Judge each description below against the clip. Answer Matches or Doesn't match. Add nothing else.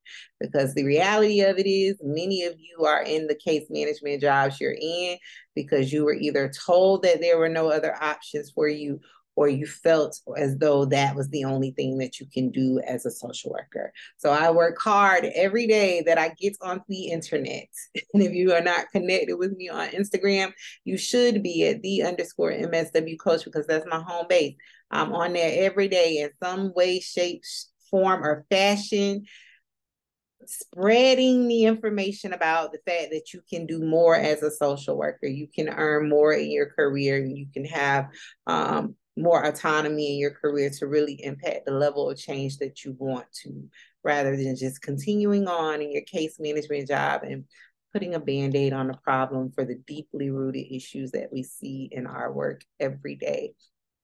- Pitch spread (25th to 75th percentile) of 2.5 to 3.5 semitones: Doesn't match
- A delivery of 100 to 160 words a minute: Doesn't match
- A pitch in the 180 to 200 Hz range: Doesn't match